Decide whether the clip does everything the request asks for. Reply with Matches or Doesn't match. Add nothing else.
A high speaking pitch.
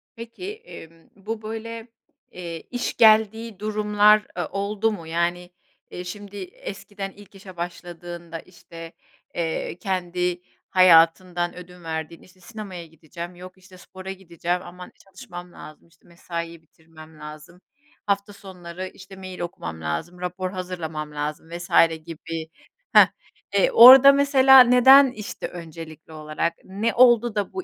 Doesn't match